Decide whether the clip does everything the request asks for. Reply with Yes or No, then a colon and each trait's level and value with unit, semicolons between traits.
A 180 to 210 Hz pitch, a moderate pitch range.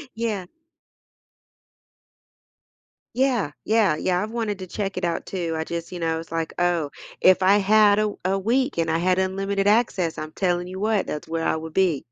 Yes: medium, 185 Hz; average, 3.7 semitones